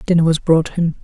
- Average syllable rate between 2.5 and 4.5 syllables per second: No, 5.8 syllables/s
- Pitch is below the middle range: No, medium, 165 Hz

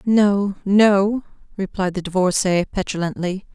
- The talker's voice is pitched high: Yes, high, 195 Hz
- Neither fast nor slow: No, slow, 100 wpm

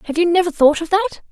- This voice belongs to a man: No, female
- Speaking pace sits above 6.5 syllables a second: Yes, 8.3 syllables/s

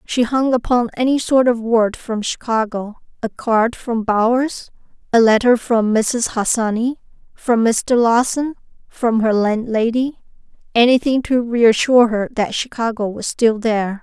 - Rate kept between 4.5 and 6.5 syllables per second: No, 4.3 syllables/s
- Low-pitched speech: No, high, 230 Hz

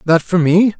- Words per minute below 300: Yes, fast, 230 wpm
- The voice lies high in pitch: No, medium, 180 Hz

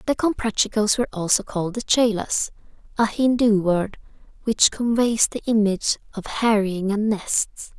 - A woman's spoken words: Yes, female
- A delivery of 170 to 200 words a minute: No, average, 140 wpm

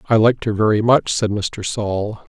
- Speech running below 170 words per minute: No, fast, 205 wpm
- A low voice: Yes, low, 105 Hz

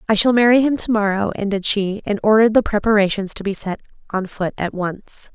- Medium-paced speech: No, fast, 215 wpm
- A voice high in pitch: Yes, high, 210 Hz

